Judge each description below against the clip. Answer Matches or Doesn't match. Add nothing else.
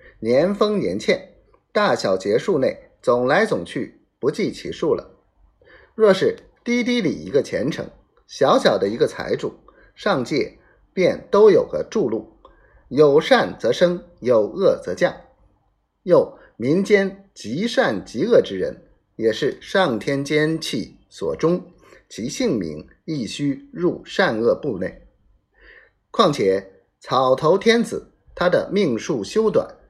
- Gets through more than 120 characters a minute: Matches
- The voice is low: Doesn't match